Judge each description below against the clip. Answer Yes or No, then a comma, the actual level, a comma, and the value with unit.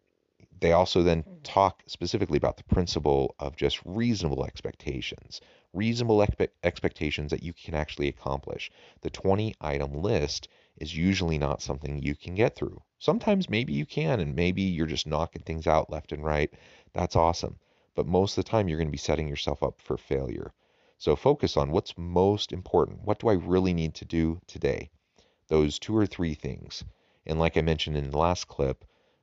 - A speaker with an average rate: Yes, average, 185 wpm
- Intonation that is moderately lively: Yes, average, 4.1 semitones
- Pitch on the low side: Yes, very low, 80 Hz